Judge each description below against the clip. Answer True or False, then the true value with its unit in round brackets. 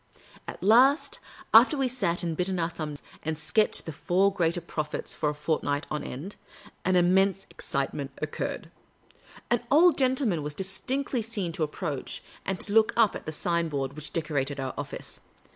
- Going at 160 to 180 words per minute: True (175 wpm)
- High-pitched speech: False (175 Hz)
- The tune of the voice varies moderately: False (5.7 semitones)